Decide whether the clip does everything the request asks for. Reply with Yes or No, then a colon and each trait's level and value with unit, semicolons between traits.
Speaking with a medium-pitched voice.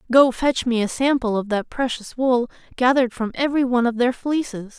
No: high, 245 Hz